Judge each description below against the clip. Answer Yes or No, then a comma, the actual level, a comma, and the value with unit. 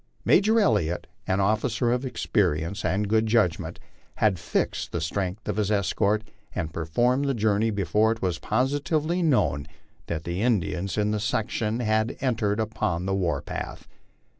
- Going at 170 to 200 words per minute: No, average, 160 wpm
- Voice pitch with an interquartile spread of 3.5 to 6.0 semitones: Yes, average, 3.9 semitones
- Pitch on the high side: No, low, 105 Hz